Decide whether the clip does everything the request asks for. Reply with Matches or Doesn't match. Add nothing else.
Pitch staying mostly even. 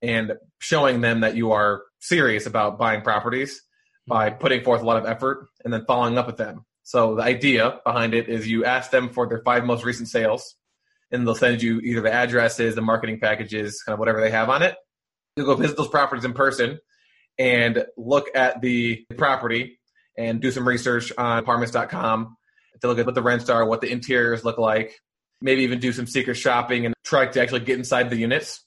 Matches